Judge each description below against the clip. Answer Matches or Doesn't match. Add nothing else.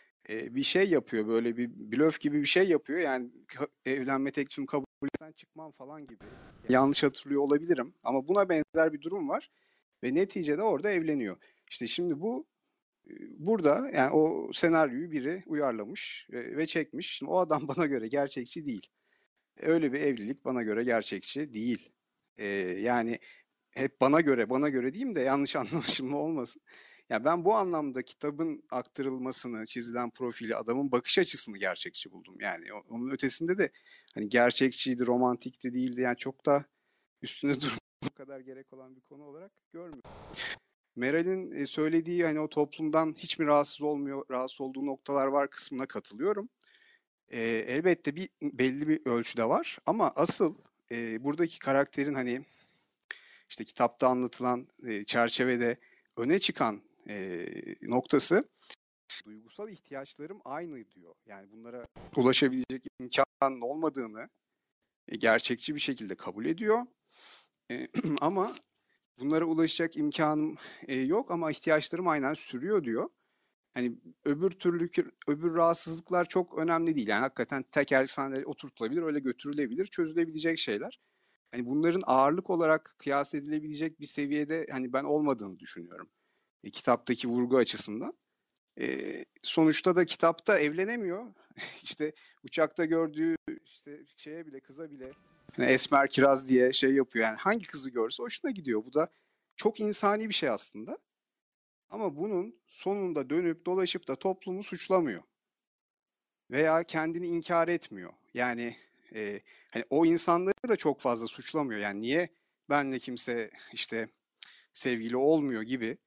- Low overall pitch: Doesn't match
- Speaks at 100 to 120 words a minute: Doesn't match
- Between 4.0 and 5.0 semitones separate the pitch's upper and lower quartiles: Matches